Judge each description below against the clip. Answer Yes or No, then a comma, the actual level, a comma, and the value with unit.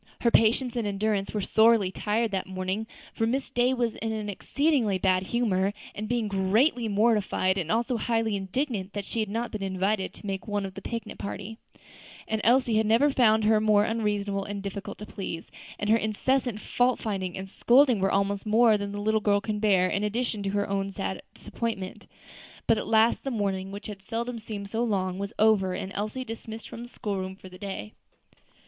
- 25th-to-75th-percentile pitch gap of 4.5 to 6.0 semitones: No, narrow, 2.6 semitones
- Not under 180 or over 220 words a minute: Yes, average, 200 wpm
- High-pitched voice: Yes, high, 210 Hz